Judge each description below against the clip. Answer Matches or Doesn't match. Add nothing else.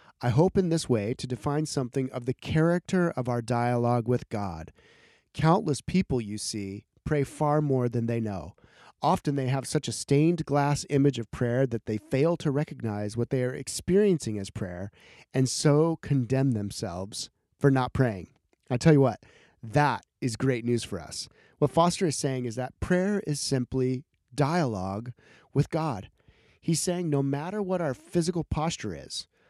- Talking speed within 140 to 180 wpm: Matches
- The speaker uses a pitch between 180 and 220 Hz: Doesn't match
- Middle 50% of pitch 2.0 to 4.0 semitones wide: Doesn't match